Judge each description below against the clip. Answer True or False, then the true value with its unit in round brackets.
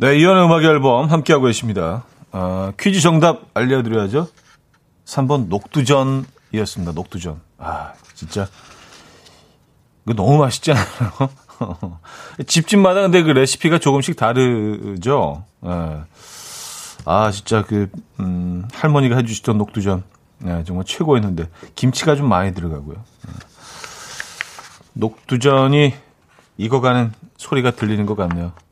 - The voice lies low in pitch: True (120 Hz)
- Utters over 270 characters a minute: False (255 characters per minute)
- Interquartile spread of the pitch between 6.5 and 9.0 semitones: True (7.0 semitones)